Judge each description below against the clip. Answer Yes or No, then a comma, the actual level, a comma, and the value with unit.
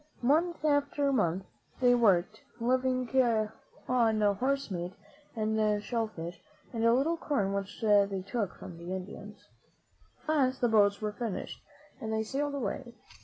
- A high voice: Yes, high, 220 Hz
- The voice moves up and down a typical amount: Yes, average, 4.2 semitones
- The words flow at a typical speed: Yes, average, 150 wpm